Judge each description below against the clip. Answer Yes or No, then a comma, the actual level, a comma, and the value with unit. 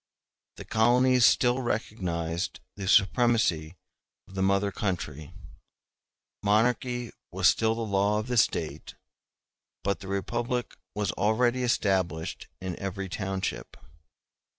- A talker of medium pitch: No, low, 100 Hz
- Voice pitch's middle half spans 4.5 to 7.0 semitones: No, average, 3.9 semitones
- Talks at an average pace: No, slow, 110 wpm